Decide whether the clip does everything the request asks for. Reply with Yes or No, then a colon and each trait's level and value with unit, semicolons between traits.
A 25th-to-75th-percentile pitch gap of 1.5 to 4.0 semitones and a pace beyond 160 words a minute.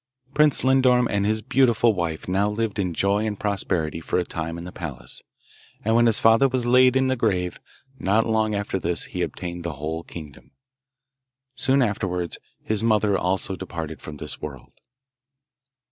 No: average, 4.9 semitones; average, 170 wpm